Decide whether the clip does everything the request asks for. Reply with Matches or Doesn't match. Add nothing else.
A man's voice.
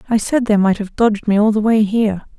Doesn't match